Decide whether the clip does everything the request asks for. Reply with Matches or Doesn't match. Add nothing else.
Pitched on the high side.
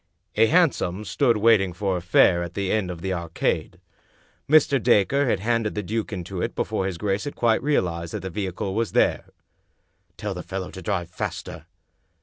Doesn't match